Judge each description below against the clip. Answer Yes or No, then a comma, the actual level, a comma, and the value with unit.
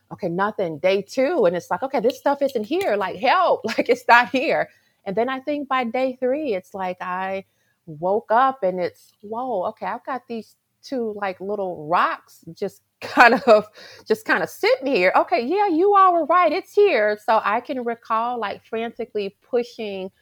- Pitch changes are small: No, average, 5.2 semitones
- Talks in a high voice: Yes, high, 230 Hz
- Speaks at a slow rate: No, average, 190 wpm